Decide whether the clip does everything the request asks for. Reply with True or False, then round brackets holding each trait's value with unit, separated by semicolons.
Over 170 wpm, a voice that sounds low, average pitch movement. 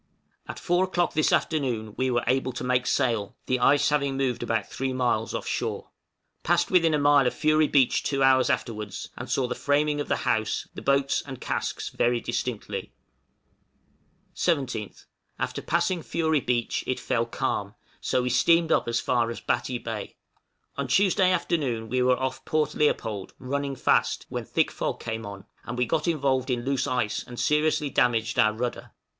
True (180 wpm; 130 Hz; 3.7 semitones)